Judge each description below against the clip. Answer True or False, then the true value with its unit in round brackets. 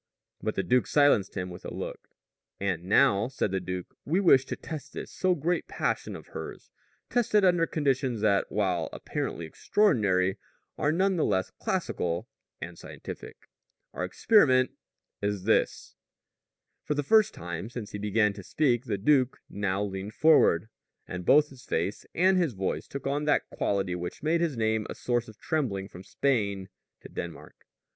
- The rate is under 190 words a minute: True (170 wpm)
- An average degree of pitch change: False (7.5 semitones)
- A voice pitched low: True (110 Hz)